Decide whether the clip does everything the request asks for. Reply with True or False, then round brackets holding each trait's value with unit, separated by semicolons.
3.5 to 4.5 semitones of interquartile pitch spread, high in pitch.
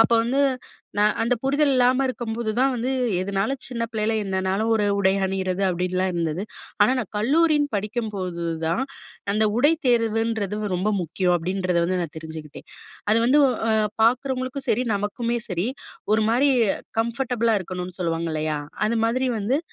False (4.9 semitones; 215 Hz)